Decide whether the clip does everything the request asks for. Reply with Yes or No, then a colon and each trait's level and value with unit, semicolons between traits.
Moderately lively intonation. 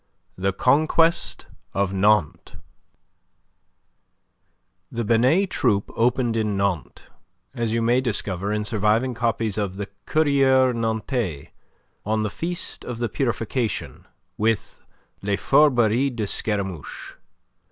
Yes: average, 3.7 semitones